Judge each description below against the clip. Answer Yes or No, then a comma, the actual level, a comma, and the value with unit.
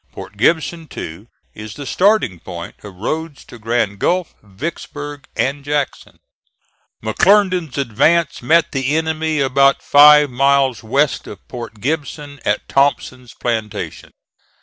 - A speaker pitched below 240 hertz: Yes, medium, 140 Hz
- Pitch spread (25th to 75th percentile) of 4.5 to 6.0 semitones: Yes, average, 5.3 semitones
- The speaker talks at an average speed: No, slow, 125 wpm